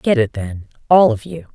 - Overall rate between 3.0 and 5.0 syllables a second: Yes, 4.7 syllables/s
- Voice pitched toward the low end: No, medium, 175 Hz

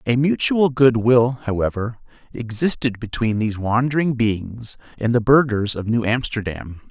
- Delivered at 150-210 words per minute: No, average, 140 wpm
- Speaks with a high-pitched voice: No, low, 120 Hz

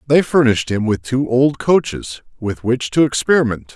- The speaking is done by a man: Yes, male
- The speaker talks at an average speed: Yes, average, 175 wpm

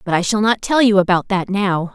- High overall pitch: Yes, high, 195 Hz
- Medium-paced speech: No, fast, 280 wpm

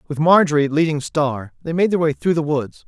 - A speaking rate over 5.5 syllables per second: No, 5.4 syllables/s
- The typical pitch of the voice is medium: Yes, medium, 155 Hz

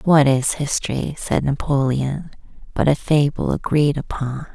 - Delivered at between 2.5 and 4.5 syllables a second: Yes, 4.3 syllables/s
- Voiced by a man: No, female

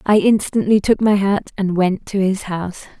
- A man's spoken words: No, female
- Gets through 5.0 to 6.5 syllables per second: No, 4.8 syllables/s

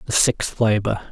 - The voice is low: Yes, low, 105 Hz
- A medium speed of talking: Yes, average, 160 wpm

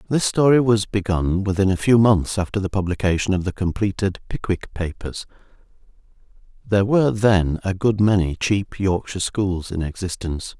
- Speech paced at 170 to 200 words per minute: No, average, 155 wpm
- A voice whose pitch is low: Yes, low, 100 Hz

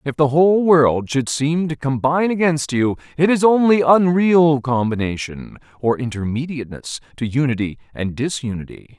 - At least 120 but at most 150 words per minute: Yes, average, 140 wpm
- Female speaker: No, male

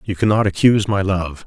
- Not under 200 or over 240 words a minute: Yes, fast, 205 wpm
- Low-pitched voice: Yes, low, 100 Hz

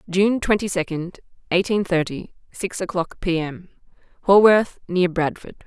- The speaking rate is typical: No, slow, 115 wpm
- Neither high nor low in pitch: Yes, medium, 180 Hz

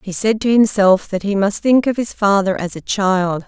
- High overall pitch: Yes, high, 200 Hz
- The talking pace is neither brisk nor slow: No, fast, 240 wpm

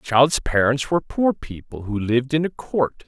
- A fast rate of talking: No, average, 195 wpm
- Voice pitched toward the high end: No, low, 135 Hz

